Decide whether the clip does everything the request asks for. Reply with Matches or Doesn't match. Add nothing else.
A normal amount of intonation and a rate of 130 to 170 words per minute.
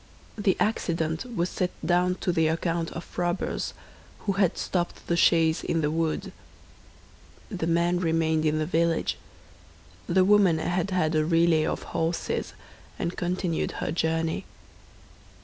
Doesn't match